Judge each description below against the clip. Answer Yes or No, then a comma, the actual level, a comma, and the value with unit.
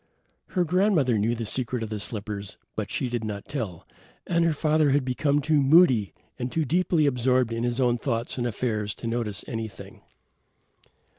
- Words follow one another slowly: No, average, 175 wpm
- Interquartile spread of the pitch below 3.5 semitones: No, average, 4.7 semitones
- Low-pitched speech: Yes, low, 125 Hz